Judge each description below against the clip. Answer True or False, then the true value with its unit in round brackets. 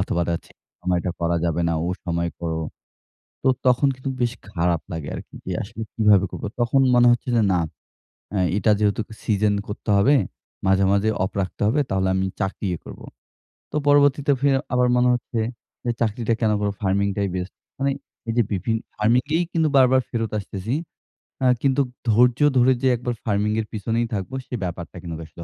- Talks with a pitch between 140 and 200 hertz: False (105 Hz)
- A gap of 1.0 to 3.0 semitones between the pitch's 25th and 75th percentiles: False (4.5 semitones)